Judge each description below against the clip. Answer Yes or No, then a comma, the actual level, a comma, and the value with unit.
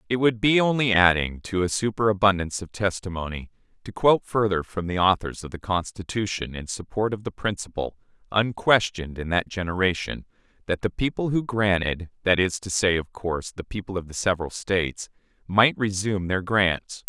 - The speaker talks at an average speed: Yes, average, 165 wpm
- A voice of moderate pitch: No, very low, 95 Hz